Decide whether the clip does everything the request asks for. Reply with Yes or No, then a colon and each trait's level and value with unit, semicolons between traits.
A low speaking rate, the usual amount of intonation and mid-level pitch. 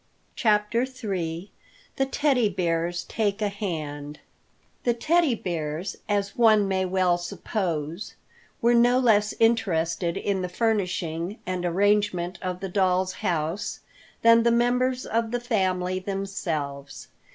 No: slow, 125 wpm; average, 4.5 semitones; high, 195 Hz